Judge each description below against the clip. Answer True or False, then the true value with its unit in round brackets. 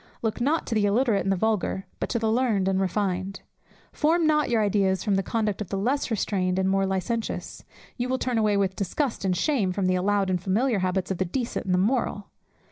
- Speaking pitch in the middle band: False (205 Hz)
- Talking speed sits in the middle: False (225 wpm)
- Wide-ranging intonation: False (3.7 semitones)